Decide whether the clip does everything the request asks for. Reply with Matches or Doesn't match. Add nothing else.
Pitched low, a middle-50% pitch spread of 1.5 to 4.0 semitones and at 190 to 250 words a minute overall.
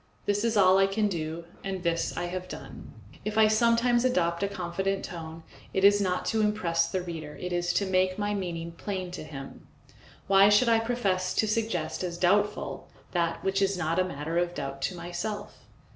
Doesn't match